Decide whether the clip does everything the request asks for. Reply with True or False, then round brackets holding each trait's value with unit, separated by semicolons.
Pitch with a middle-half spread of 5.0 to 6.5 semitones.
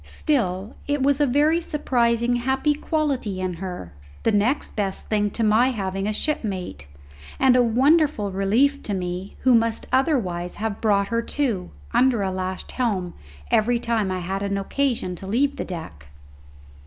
True (5.5 semitones)